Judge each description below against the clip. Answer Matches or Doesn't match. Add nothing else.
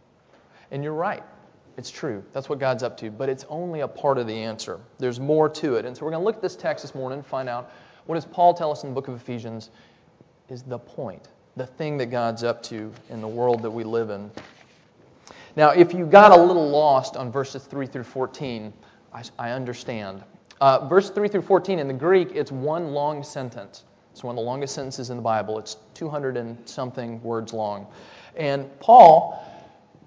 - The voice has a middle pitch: Doesn't match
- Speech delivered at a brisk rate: Matches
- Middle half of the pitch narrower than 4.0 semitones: Doesn't match